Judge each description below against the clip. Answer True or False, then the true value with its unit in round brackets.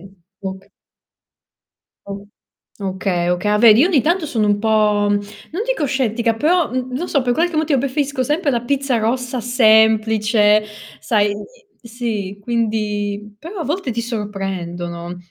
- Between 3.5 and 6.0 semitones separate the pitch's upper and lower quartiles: True (4.2 semitones)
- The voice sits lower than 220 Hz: False (225 Hz)